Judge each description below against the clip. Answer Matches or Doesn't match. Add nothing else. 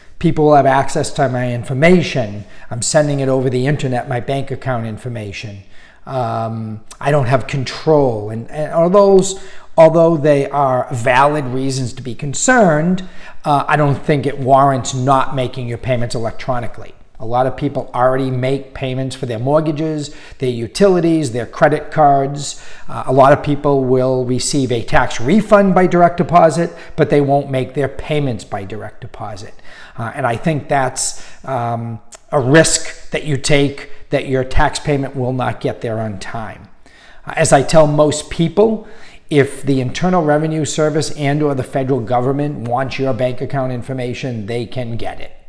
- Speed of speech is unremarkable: Matches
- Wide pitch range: Doesn't match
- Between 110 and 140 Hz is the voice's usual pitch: Matches